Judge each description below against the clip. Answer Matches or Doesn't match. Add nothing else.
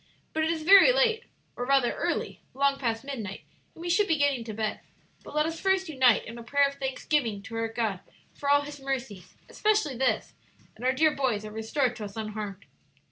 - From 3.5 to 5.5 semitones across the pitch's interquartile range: Matches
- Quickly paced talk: Matches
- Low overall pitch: Doesn't match